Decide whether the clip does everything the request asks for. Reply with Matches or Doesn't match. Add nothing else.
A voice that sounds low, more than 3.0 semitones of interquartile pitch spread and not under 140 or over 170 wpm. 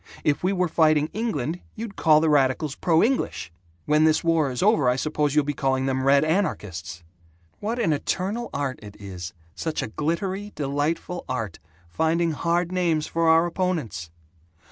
Doesn't match